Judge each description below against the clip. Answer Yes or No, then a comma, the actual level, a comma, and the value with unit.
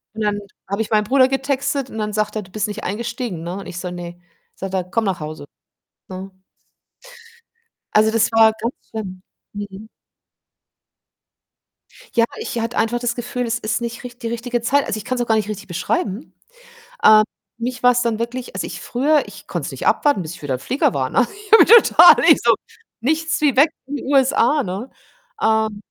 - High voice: Yes, high, 225 Hz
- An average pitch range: Yes, average, 3.6 semitones